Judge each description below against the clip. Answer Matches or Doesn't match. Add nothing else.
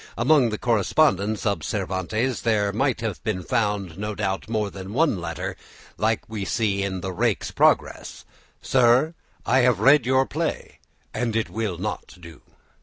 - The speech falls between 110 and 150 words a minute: Doesn't match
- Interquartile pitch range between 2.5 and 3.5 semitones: Doesn't match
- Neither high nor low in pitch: Doesn't match